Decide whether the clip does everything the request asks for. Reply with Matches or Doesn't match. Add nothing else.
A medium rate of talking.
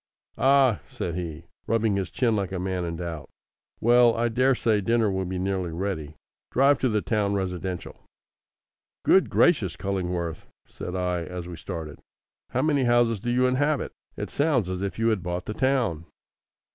Matches